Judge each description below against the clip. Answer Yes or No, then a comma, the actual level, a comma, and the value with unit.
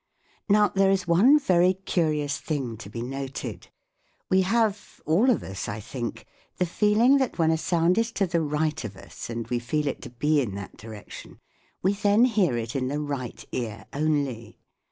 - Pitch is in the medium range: Yes, medium, 155 Hz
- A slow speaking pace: No, average, 190 wpm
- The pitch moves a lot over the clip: Yes, wide, 7.9 semitones